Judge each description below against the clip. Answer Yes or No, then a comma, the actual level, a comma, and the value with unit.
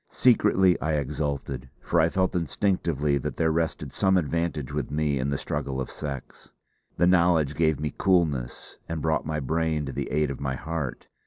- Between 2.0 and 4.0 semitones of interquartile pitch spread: Yes, average, 2.9 semitones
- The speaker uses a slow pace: No, average, 180 wpm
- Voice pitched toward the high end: No, very low, 75 Hz